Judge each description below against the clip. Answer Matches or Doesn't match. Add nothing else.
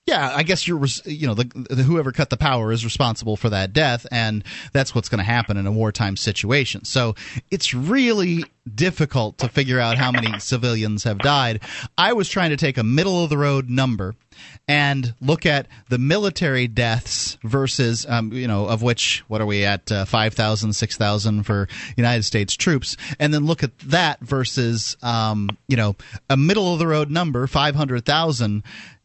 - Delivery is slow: Doesn't match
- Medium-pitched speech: Doesn't match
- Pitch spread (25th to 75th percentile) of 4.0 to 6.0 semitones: Matches